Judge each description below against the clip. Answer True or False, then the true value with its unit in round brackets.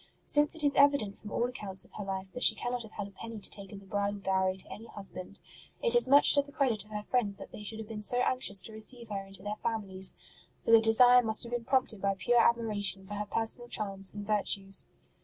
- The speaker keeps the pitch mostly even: False (3.5 semitones)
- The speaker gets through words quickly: True (250 wpm)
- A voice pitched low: False (215 Hz)